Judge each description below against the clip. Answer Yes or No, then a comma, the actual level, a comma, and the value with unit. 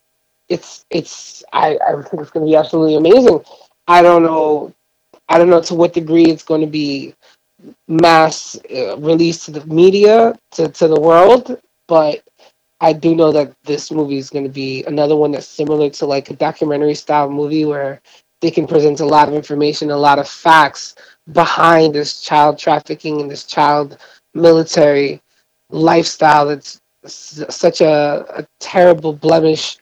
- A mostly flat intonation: Yes, narrow, 2.0 semitones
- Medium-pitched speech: Yes, medium, 155 Hz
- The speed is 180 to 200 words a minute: No, average, 165 wpm